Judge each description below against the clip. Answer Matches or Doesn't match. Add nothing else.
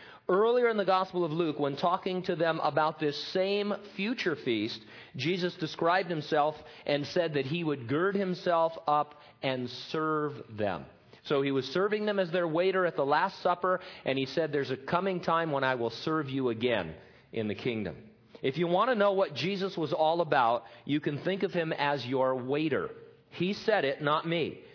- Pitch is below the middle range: Doesn't match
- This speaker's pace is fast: Doesn't match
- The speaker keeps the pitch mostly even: Doesn't match